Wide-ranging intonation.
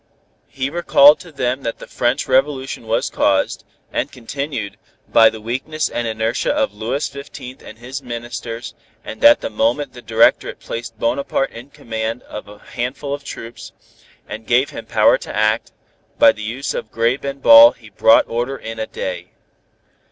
No: average, 3.7 semitones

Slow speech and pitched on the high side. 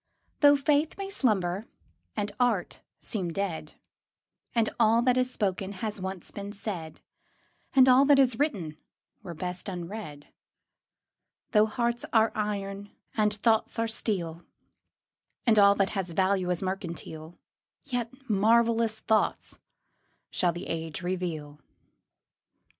Yes: slow, 125 wpm; high, 205 Hz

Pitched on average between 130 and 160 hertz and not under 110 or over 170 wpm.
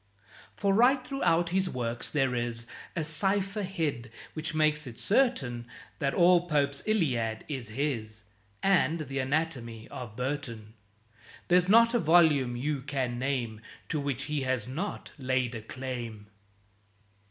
Yes: medium, 140 Hz; average, 140 wpm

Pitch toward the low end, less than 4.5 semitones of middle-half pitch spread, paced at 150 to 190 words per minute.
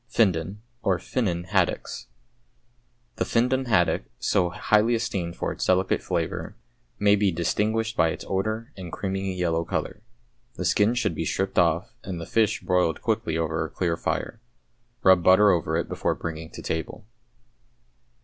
Yes: very low, 95 Hz; average, 3.9 semitones; average, 155 wpm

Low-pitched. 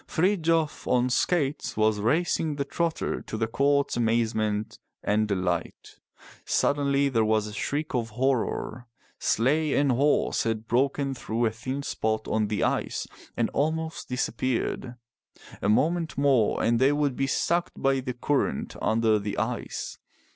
Yes: low, 125 Hz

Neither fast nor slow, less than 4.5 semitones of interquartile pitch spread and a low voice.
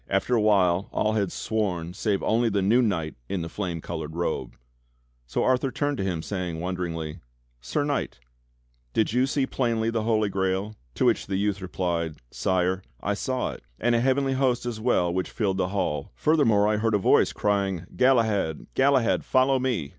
No: average, 185 wpm; average, 4.9 semitones; low, 100 Hz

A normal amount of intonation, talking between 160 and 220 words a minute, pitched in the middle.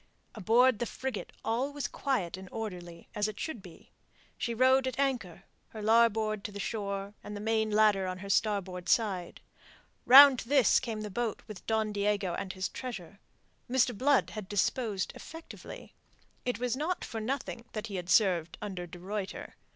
No: average, 3.8 semitones; average, 175 wpm; high, 215 Hz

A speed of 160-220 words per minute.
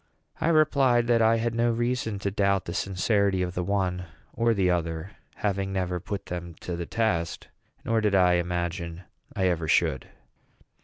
Yes: average, 170 wpm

